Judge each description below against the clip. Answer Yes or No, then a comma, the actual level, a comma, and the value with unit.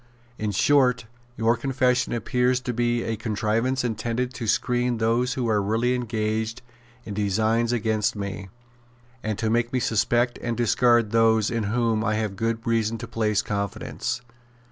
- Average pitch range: No, narrow, 2.0 semitones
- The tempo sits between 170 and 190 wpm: No, average, 155 wpm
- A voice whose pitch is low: Yes, low, 115 Hz